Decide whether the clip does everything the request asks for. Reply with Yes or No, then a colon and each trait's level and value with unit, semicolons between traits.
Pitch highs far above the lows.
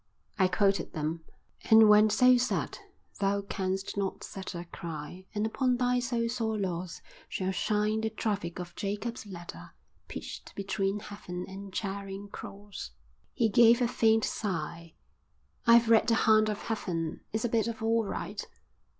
No: average, 2.9 semitones